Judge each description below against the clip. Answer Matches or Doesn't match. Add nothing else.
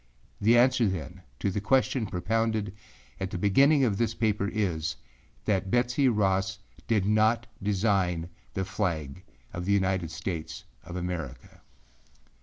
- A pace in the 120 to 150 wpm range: Matches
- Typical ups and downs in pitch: Matches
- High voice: Doesn't match